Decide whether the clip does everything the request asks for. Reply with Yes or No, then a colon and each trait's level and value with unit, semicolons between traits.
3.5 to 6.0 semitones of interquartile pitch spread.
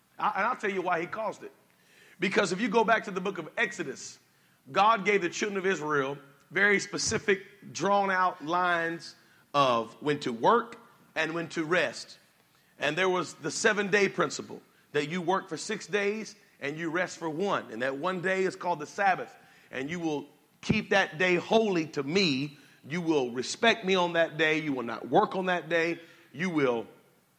Yes: average, 4.3 semitones